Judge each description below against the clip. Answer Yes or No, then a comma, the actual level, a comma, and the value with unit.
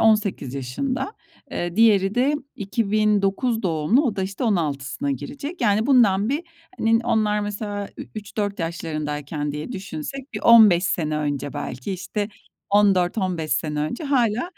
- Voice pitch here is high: Yes, high, 200 Hz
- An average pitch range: No, wide, 6.0 semitones